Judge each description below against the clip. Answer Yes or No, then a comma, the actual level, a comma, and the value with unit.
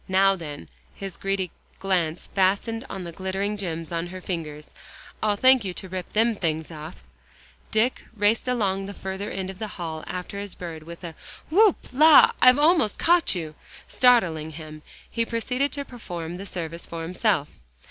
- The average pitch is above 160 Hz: Yes, high, 190 Hz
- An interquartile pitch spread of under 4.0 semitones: No, average, 4.7 semitones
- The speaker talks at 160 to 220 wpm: Yes, average, 170 wpm